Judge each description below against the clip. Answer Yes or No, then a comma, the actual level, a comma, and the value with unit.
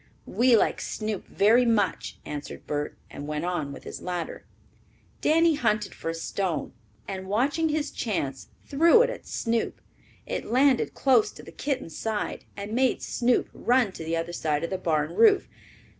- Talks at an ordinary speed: Yes, average, 170 wpm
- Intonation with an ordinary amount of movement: No, wide, 7.6 semitones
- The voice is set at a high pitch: Yes, high, 210 Hz